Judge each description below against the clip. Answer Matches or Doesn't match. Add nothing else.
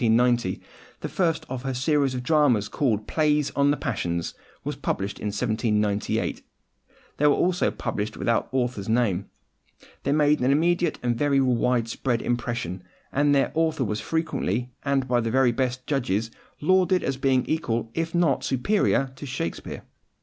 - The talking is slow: Doesn't match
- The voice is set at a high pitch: Doesn't match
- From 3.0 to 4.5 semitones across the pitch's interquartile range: Matches